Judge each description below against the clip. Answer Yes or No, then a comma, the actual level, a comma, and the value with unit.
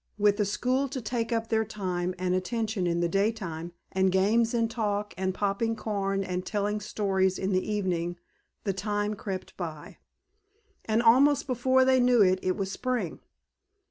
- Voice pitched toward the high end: Yes, high, 205 Hz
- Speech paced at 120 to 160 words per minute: No, average, 170 wpm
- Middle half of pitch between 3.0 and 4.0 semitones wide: Yes, average, 3.3 semitones